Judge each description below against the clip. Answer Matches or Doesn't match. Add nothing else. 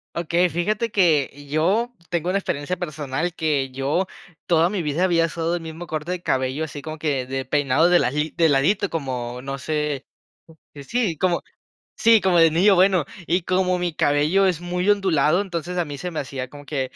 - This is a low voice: Doesn't match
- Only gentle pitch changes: Doesn't match